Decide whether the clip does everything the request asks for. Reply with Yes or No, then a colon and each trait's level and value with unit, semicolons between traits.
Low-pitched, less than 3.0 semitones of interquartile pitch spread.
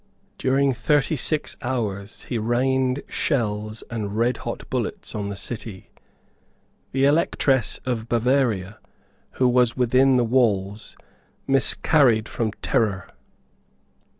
No: low, 120 Hz; average, 3.5 semitones